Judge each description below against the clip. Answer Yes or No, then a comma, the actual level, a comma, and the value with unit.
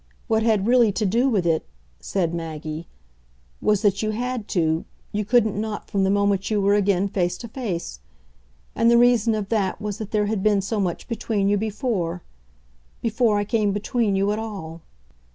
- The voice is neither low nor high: No, high, 205 Hz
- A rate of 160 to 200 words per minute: Yes, average, 190 wpm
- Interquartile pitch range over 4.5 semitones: No, narrow, 2.5 semitones